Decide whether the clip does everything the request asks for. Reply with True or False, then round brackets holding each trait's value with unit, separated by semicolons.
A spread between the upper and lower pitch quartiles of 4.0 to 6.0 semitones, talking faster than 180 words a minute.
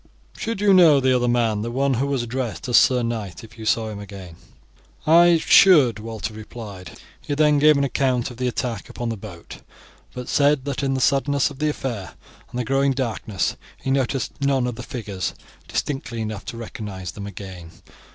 True (4.3 semitones; 195 wpm)